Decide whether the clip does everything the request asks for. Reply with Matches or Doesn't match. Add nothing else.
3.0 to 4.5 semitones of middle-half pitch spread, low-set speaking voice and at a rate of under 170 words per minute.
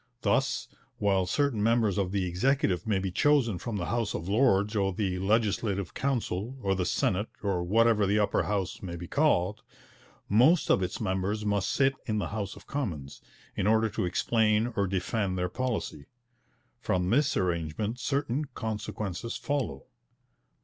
Matches